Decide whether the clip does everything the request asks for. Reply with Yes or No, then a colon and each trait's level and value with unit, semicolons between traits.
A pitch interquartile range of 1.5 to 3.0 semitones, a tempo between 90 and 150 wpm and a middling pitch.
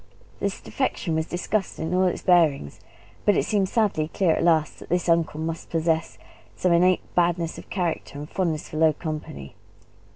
No: narrow, 2.4 semitones; average, 175 wpm; medium, 170 Hz